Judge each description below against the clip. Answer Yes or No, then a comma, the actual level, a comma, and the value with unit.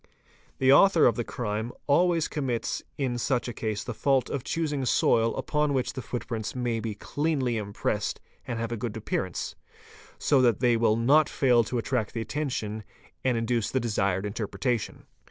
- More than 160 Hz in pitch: No, low, 120 Hz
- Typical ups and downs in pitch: Yes, average, 3.3 semitones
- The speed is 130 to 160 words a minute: No, average, 175 wpm